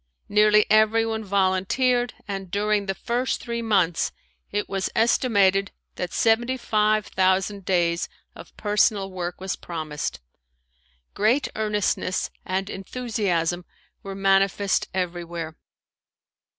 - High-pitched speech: Yes, high, 200 Hz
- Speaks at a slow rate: Yes, slow, 105 wpm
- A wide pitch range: No, narrow, 2.6 semitones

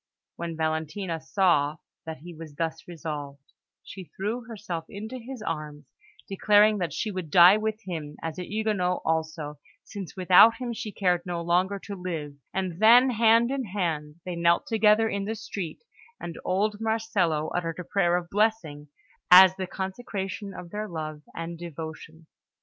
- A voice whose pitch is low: No, medium, 180 Hz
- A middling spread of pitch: Yes, average, 4.5 semitones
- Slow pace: No, average, 160 wpm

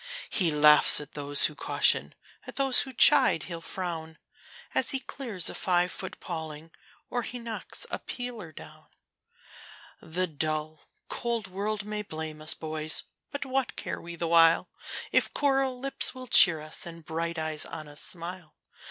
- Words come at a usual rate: Yes, average, 160 wpm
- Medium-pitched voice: Yes, medium, 170 Hz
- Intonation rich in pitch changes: Yes, wide, 6.6 semitones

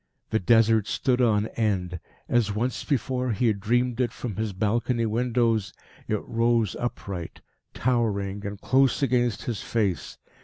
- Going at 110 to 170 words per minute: Yes, average, 145 wpm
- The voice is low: Yes, low, 115 Hz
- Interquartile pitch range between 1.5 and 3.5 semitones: Yes, average, 3.0 semitones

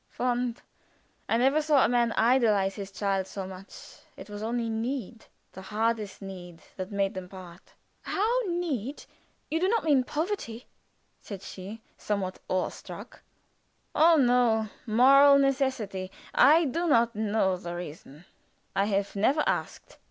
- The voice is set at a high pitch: Yes, high, 225 Hz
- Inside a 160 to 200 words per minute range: No, average, 145 wpm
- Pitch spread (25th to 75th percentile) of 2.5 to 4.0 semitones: No, wide, 5.6 semitones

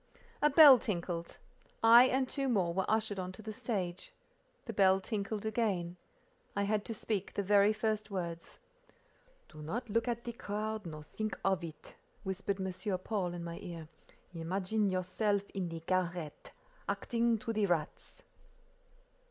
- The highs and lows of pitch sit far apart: No, average, 3.7 semitones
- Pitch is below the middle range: No, high, 200 Hz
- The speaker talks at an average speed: Yes, average, 155 wpm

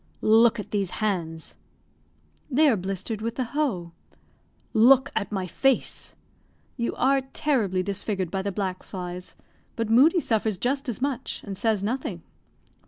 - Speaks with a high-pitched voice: Yes, high, 215 Hz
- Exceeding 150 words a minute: No, average, 145 wpm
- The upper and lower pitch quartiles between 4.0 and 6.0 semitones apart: Yes, average, 4.9 semitones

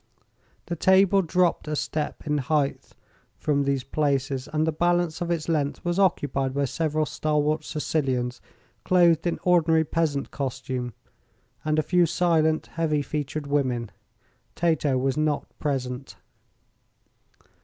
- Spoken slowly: Yes, slow, 130 wpm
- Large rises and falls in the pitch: No, average, 3.0 semitones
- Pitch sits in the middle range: Yes, medium, 150 Hz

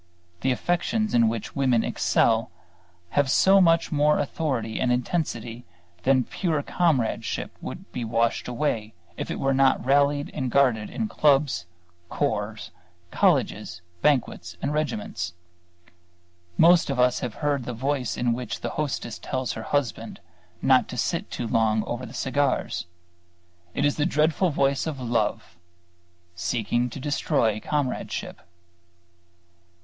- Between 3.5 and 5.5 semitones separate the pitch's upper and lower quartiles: Yes, average, 4.0 semitones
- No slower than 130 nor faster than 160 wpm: Yes, slow, 135 wpm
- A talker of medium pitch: No, low, 130 Hz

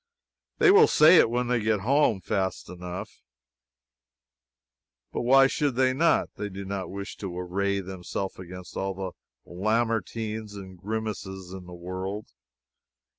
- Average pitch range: Yes, average, 3.6 semitones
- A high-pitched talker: No, low, 100 Hz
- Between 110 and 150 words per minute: Yes, average, 140 wpm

